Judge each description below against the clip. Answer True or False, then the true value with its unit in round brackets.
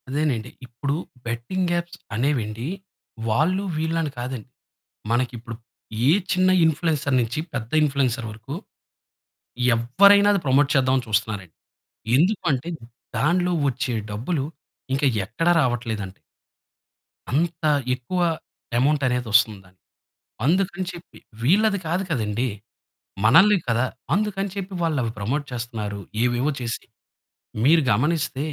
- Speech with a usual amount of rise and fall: False (6.0 semitones)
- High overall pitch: False (135 Hz)